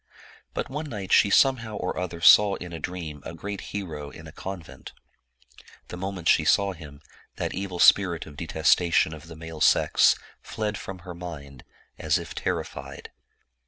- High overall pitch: No, very low, 90 Hz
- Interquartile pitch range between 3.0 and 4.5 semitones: Yes, average, 3.6 semitones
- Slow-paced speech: No, average, 165 wpm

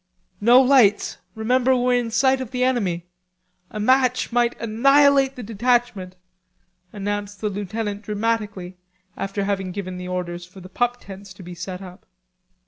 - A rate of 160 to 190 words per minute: No, average, 150 wpm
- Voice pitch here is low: No, high, 210 Hz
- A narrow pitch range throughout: No, average, 4.3 semitones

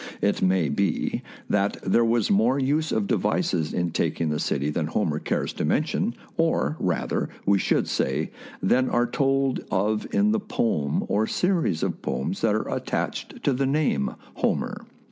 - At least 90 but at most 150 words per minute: No, average, 165 wpm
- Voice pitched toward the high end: No, low, 105 Hz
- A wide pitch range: Yes, wide, 8.1 semitones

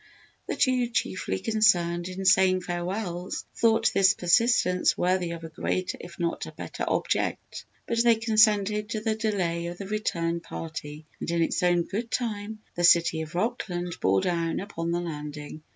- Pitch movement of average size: Yes, average, 4.0 semitones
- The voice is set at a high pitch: No, medium, 180 Hz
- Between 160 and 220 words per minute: Yes, average, 170 wpm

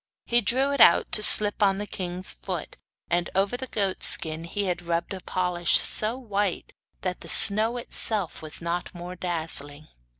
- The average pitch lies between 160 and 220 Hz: Yes, medium, 185 Hz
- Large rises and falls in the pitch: No, average, 3.6 semitones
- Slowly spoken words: No, average, 175 wpm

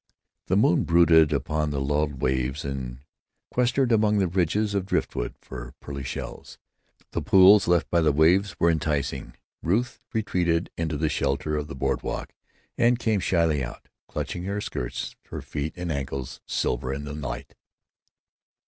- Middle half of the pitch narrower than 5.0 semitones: No, average, 5.3 semitones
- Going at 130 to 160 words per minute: Yes, average, 155 wpm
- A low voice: Yes, very low, 80 Hz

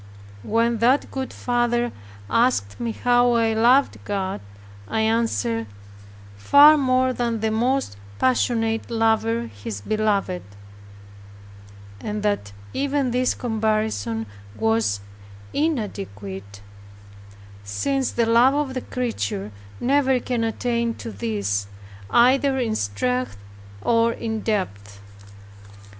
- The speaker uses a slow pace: Yes, slow, 105 wpm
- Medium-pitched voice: No, high, 225 Hz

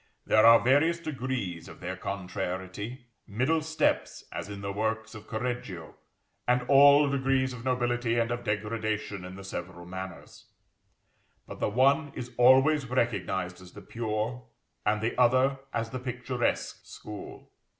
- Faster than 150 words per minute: No, average, 145 wpm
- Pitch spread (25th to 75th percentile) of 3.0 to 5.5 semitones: Yes, average, 4.3 semitones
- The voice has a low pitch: Yes, low, 115 Hz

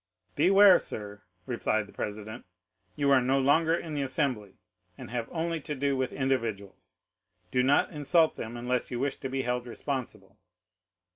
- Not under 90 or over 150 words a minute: No, average, 160 wpm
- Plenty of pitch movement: No, average, 3.5 semitones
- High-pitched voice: No, low, 130 Hz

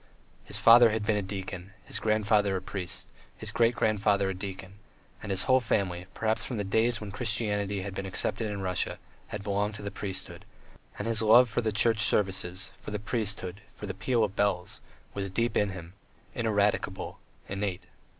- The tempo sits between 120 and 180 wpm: No, average, 190 wpm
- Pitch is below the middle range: Yes, low, 105 Hz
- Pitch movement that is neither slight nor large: No, narrow, 2.2 semitones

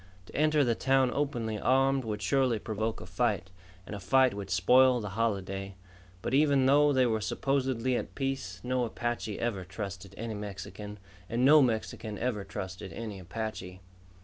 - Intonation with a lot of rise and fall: No, average, 4.8 semitones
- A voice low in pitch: Yes, low, 115 Hz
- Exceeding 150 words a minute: Yes, average, 165 wpm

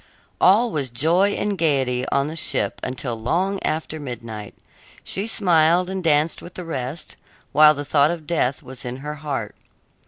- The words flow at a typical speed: Yes, average, 165 wpm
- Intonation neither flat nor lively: Yes, average, 4.7 semitones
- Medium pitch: Yes, medium, 150 Hz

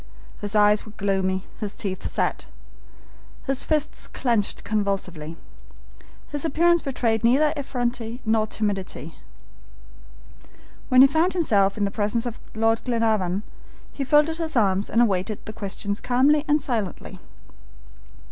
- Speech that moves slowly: Yes, slow, 130 wpm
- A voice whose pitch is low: No, high, 225 Hz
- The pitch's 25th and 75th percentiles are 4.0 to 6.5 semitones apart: Yes, average, 5.1 semitones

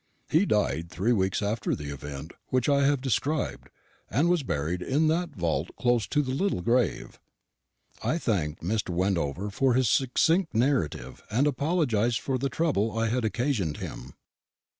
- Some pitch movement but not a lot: No, wide, 7.4 semitones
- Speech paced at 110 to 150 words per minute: No, average, 160 wpm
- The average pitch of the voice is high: No, low, 115 Hz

